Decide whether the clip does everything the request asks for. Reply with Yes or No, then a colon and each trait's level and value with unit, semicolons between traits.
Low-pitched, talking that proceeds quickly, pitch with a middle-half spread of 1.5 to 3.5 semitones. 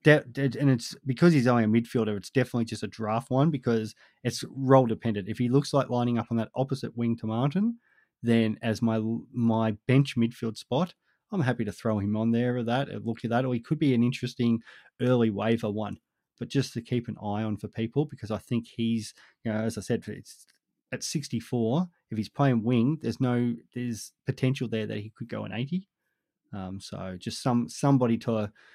Yes: low, 120 Hz; fast, 210 wpm; average, 2.8 semitones